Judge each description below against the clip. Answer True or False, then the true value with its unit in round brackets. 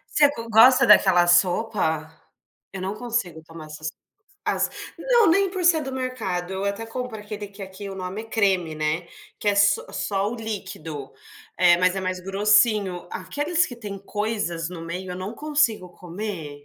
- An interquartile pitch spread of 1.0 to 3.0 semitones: False (4.2 semitones)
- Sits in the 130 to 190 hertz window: False (200 Hz)